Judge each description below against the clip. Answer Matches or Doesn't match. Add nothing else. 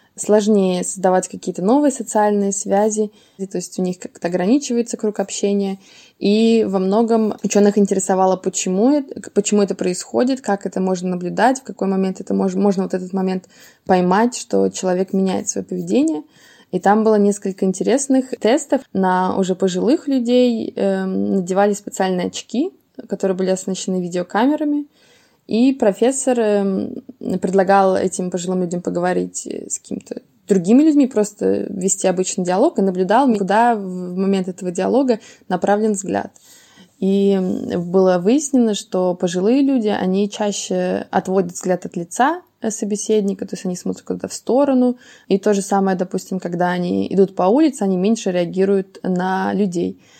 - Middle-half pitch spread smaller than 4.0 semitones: Matches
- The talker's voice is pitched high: Matches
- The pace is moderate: Matches